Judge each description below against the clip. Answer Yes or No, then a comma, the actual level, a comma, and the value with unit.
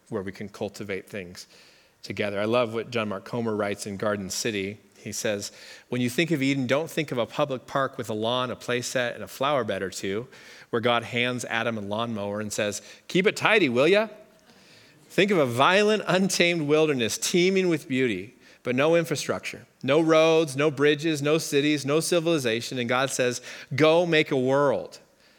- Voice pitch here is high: No, low, 135 Hz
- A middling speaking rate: Yes, average, 190 wpm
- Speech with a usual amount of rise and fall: No, wide, 5.8 semitones